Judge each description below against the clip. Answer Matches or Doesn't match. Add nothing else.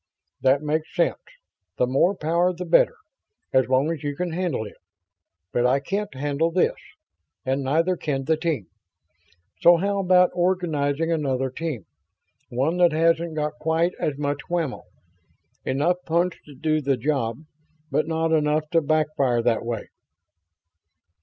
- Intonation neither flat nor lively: Matches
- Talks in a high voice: Doesn't match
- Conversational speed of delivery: Matches